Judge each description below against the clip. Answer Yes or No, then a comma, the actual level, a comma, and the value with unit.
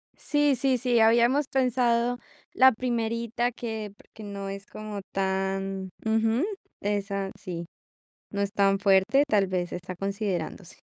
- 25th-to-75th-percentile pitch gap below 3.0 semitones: No, average, 3.5 semitones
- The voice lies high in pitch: Yes, high, 215 Hz